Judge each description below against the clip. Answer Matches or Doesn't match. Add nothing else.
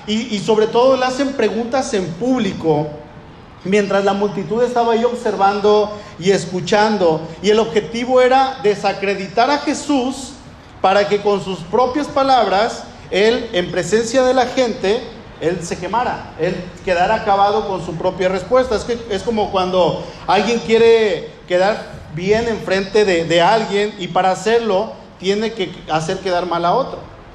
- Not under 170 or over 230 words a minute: Doesn't match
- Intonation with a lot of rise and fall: Doesn't match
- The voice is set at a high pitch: Matches